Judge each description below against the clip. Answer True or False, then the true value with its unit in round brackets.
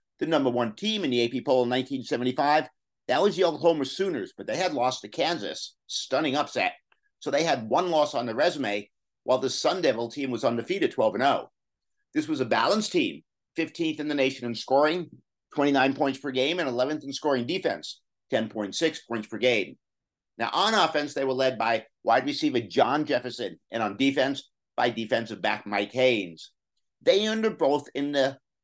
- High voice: False (135 Hz)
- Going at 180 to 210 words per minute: True (185 wpm)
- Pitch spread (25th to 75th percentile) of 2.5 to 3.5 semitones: False (5.1 semitones)